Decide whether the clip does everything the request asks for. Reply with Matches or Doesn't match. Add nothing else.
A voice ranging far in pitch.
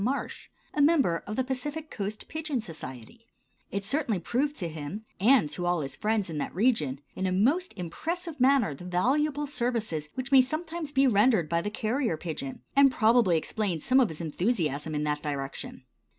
Matches